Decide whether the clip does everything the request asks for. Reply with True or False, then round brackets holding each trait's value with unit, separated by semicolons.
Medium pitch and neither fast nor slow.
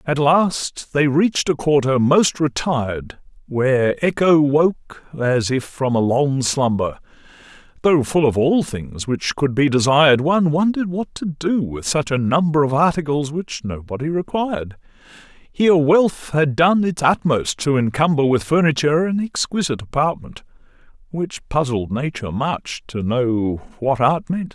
True (145 Hz; 150 wpm)